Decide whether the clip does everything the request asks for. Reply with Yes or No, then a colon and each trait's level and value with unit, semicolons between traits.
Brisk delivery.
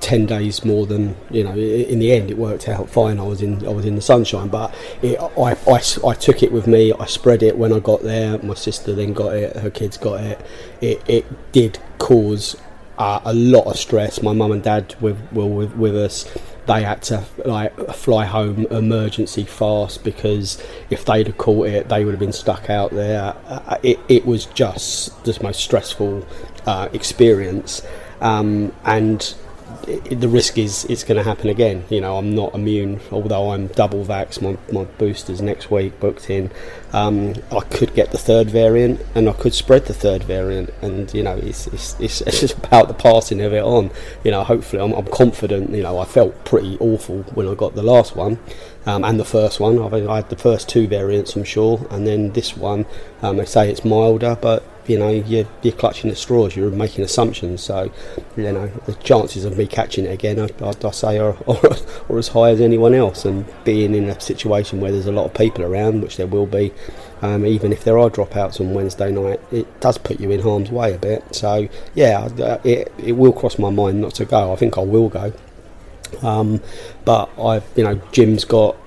Yes: fast, 210 wpm